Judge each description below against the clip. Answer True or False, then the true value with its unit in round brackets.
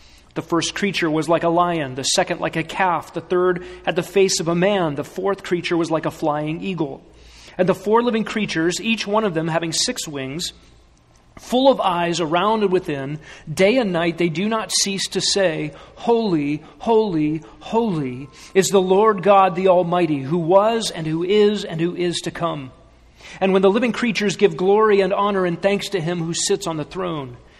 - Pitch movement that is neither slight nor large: True (3.6 semitones)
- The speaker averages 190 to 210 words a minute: True (200 wpm)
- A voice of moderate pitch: True (175 Hz)